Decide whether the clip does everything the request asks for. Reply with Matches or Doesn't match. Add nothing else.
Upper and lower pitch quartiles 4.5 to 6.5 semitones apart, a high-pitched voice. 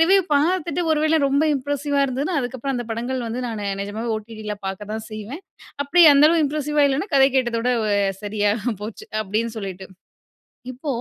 Matches